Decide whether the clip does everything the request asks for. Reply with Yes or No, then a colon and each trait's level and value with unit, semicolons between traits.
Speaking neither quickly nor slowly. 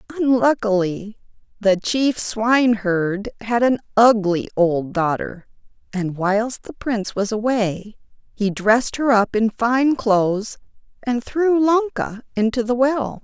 No: slow, 125 wpm